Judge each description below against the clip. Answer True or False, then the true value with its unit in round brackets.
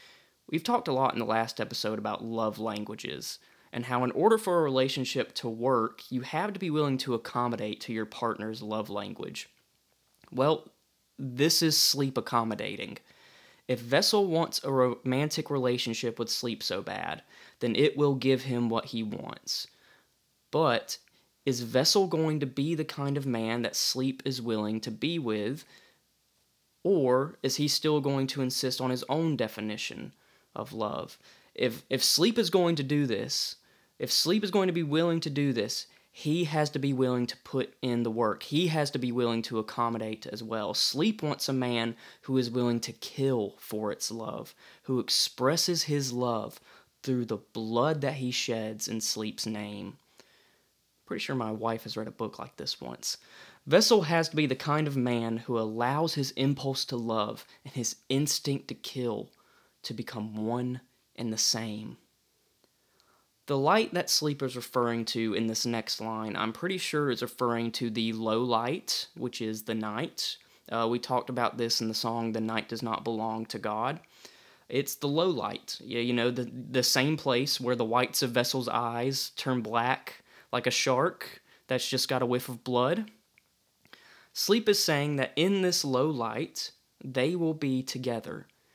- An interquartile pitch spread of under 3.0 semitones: False (3.8 semitones)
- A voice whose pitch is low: True (125 Hz)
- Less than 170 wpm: False (180 wpm)